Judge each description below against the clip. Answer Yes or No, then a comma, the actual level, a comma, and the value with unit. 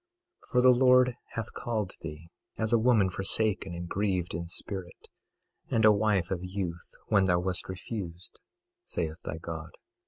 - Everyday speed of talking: Yes, average, 160 wpm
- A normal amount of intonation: Yes, average, 4.1 semitones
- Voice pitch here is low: Yes, very low, 95 Hz